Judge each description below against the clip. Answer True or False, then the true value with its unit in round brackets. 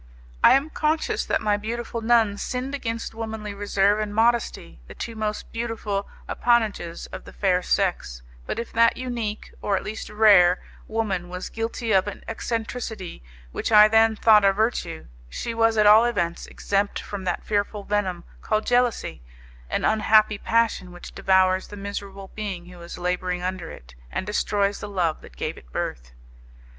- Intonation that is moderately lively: True (3.1 semitones)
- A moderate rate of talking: True (170 wpm)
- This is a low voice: False (210 Hz)